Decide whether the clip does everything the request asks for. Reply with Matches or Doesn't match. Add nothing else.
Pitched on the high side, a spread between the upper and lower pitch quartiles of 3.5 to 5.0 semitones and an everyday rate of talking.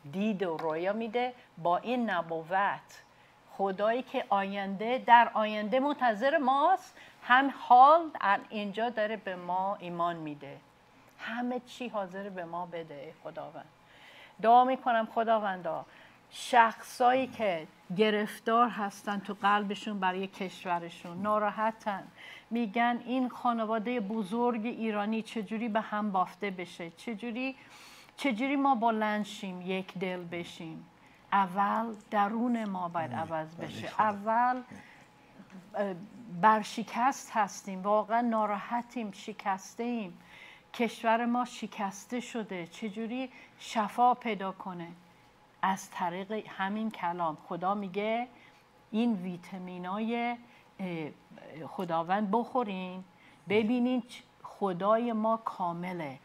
Doesn't match